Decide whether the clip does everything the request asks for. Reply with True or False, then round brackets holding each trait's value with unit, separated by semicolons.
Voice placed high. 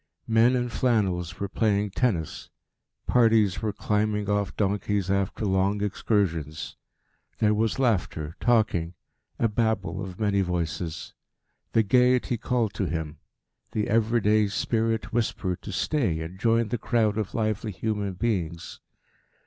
False (105 Hz)